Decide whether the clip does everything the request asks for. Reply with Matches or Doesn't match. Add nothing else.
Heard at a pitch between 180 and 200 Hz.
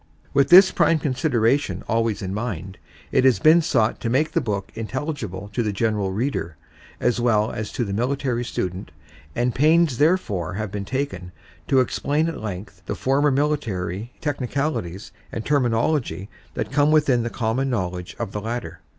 Doesn't match